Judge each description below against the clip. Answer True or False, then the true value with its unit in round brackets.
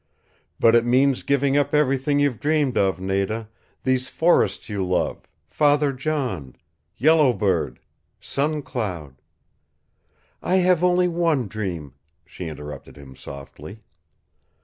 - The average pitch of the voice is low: True (130 Hz)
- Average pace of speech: False (125 wpm)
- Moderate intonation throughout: False (7.5 semitones)